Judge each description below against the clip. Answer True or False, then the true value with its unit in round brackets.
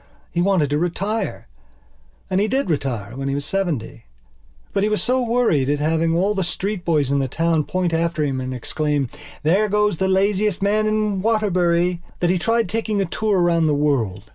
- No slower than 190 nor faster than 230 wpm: True (195 wpm)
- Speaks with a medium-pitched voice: True (175 Hz)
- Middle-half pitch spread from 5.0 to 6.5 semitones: True (5.6 semitones)